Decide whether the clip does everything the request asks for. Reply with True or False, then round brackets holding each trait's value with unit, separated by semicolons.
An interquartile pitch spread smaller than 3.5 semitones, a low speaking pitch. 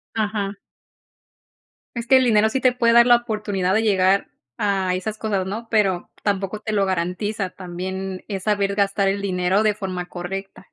False (2.4 semitones; 200 Hz)